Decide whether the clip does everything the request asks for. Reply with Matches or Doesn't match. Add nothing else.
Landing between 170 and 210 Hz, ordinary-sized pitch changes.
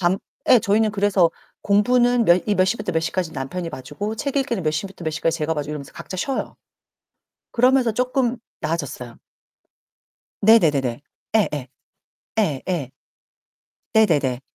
Doesn't match